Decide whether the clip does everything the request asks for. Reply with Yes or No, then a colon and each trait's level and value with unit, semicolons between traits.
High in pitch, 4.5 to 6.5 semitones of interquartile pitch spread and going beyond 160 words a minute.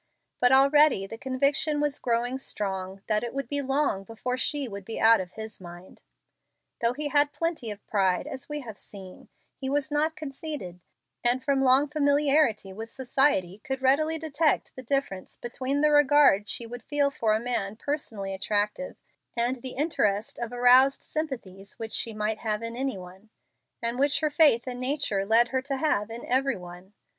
Yes: very high, 250 Hz; average, 5.1 semitones; average, 180 wpm